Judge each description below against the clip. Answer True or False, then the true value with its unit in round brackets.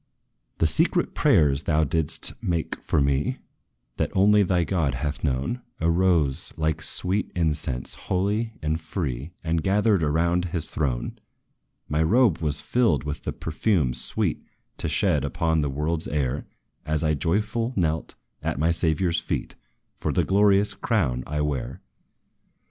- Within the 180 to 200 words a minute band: False (145 wpm)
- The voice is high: False (80 Hz)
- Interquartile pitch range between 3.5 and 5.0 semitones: True (4.0 semitones)